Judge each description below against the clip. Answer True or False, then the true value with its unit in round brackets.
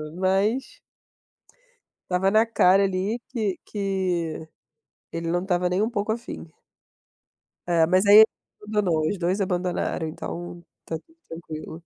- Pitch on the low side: False (185 Hz)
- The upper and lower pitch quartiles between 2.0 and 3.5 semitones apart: True (3.1 semitones)